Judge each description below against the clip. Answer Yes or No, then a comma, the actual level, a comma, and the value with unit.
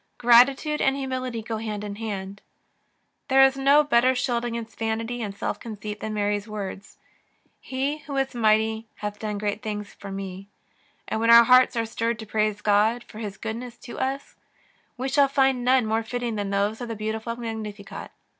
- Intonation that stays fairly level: No, average, 3.0 semitones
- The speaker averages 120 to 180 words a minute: No, average, 190 wpm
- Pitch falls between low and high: No, high, 225 Hz